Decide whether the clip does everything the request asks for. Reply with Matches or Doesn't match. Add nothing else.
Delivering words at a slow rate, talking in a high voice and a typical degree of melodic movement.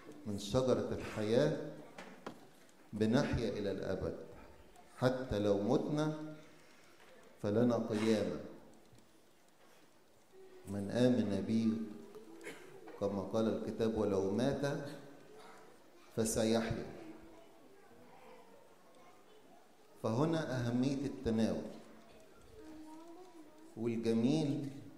Doesn't match